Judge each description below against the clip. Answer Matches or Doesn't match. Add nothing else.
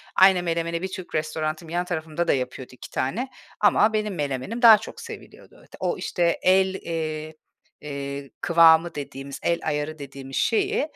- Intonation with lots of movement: Doesn't match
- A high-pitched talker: Doesn't match